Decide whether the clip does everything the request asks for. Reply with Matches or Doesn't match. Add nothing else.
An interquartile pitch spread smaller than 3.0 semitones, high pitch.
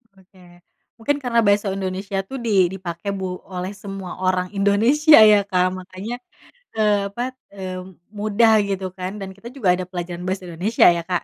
Matches